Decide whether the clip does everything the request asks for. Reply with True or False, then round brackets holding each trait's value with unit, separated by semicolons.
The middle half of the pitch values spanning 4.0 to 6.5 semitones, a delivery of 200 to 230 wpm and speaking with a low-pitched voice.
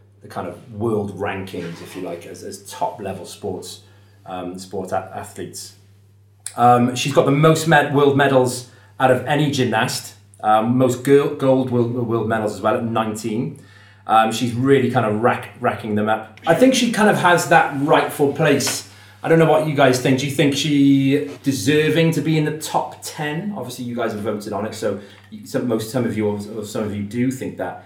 True (5.2 semitones; 205 wpm; 120 Hz)